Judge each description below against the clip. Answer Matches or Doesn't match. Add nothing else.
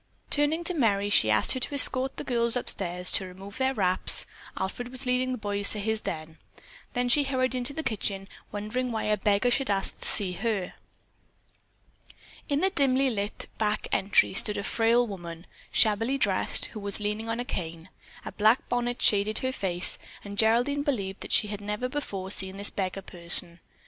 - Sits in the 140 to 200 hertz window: Doesn't match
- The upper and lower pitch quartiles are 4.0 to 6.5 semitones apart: Matches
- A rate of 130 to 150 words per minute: Doesn't match